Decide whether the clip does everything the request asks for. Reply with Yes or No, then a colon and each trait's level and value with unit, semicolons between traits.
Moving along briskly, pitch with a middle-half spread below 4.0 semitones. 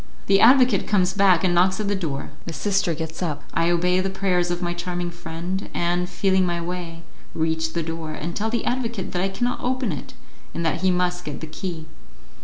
Yes: fast, 210 wpm; narrow, 2.5 semitones